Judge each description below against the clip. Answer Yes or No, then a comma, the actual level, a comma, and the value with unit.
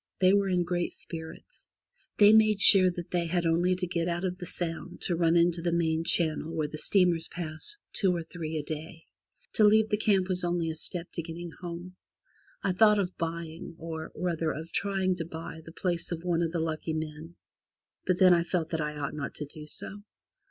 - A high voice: No, medium, 170 Hz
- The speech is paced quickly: Yes, fast, 215 wpm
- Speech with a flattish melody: Yes, narrow, 2.0 semitones